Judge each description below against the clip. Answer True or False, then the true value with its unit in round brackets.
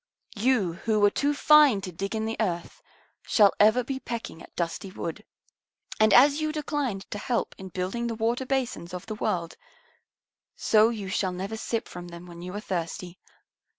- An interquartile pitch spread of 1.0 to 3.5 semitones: False (4.8 semitones)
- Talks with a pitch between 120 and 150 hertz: False (210 Hz)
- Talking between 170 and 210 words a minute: True (185 wpm)